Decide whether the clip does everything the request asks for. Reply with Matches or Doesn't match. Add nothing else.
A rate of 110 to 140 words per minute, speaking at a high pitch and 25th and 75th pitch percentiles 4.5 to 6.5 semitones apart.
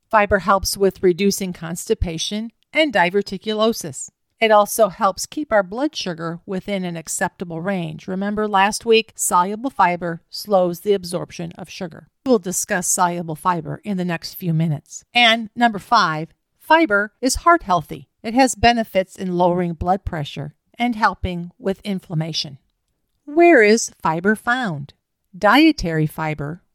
Doesn't match